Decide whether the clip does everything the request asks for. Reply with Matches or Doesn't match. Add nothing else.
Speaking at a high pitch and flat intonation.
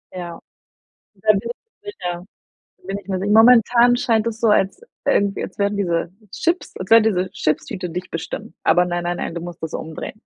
Doesn't match